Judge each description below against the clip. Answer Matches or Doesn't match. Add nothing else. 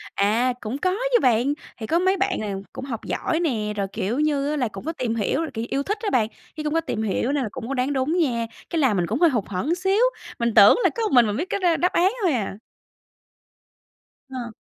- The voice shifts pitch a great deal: Matches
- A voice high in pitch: Matches